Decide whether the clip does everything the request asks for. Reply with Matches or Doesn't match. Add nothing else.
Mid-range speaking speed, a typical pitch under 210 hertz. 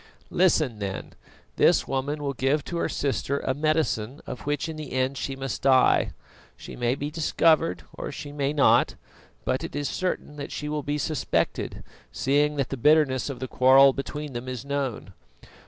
Matches